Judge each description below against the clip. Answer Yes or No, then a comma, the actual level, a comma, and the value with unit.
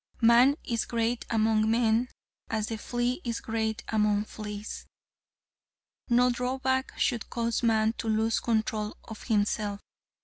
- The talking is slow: Yes, slow, 130 wpm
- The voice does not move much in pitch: Yes, narrow, 1.8 semitones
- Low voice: No, high, 225 Hz